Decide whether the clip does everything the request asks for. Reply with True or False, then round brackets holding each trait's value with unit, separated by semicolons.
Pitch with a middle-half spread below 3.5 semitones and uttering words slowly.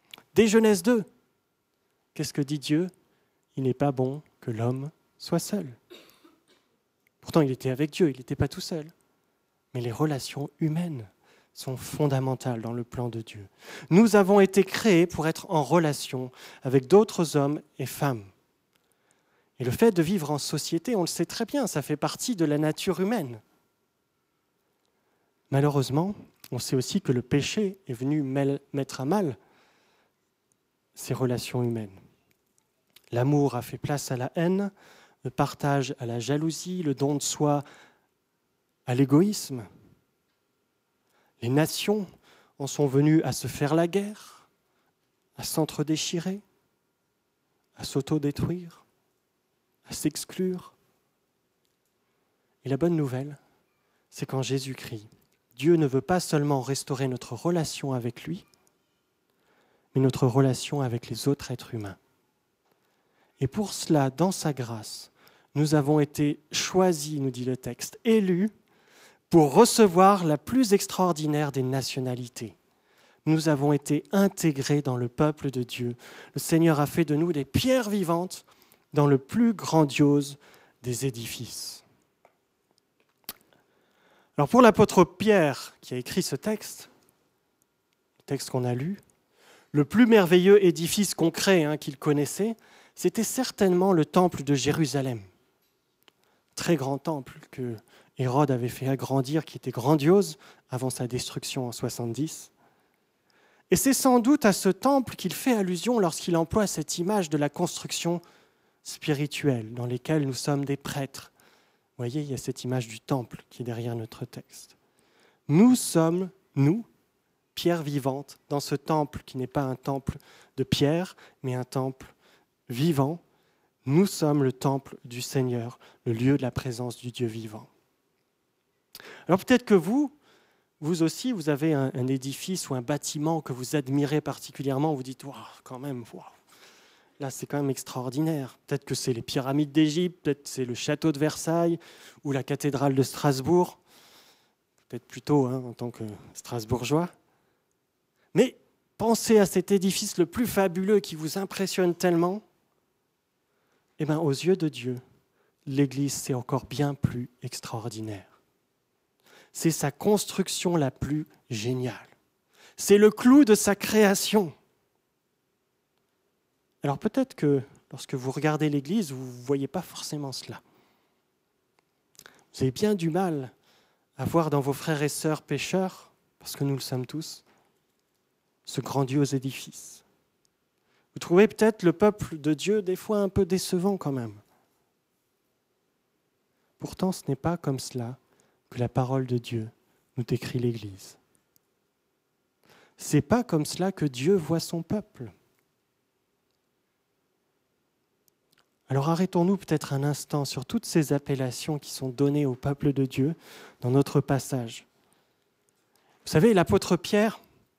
False (5.0 semitones; 140 wpm)